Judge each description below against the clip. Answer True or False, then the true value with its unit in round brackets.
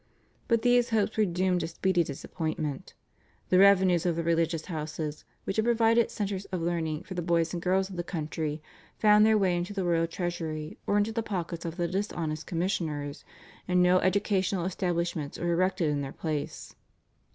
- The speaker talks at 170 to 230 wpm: True (180 wpm)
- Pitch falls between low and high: True (175 Hz)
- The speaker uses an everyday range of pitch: True (3.0 semitones)